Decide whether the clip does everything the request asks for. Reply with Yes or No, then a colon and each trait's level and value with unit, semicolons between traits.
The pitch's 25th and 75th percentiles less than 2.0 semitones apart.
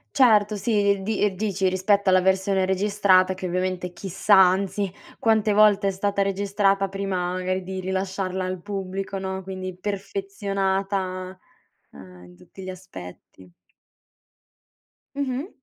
Yes: narrow, 1.4 semitones